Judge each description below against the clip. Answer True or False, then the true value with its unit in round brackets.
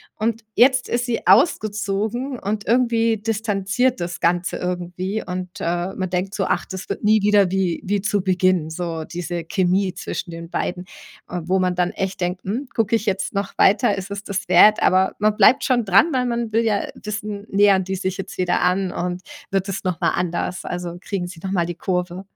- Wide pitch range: False (2.9 semitones)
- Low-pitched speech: False (195 Hz)